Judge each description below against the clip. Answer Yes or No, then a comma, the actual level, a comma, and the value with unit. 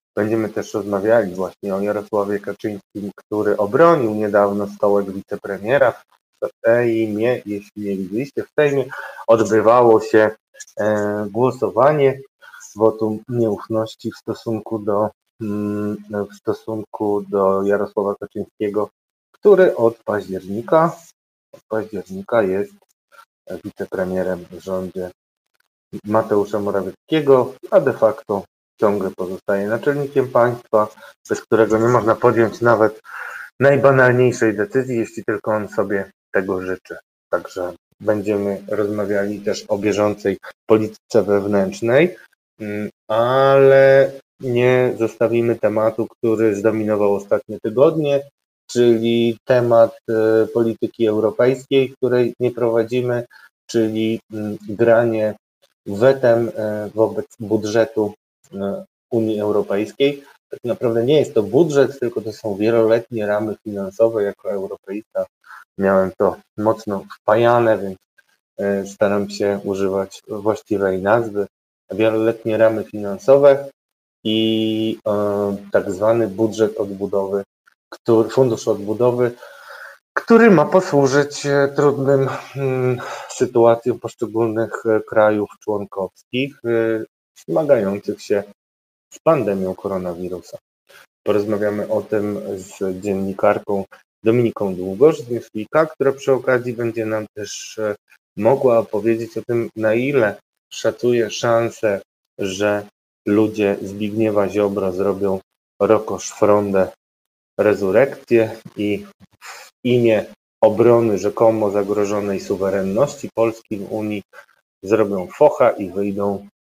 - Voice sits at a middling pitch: No, low, 110 Hz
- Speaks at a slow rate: Yes, slow, 95 wpm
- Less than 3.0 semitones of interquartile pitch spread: Yes, narrow, 2.6 semitones